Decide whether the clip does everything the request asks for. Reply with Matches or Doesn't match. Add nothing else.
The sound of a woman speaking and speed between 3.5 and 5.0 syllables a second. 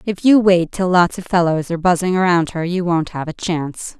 Doesn't match